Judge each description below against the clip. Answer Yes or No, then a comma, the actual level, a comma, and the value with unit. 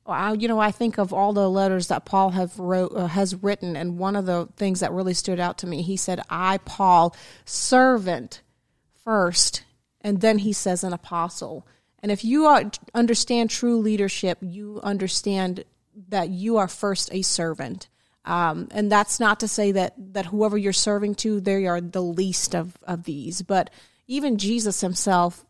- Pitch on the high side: Yes, high, 195 Hz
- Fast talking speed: No, average, 180 wpm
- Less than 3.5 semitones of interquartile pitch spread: Yes, narrow, 2.5 semitones